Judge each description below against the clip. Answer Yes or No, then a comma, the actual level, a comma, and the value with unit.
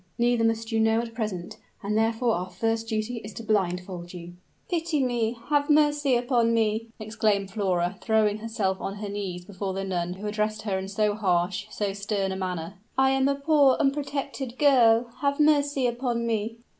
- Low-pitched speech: No, high, 220 Hz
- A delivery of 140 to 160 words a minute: No, average, 180 wpm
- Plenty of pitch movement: No, average, 3.8 semitones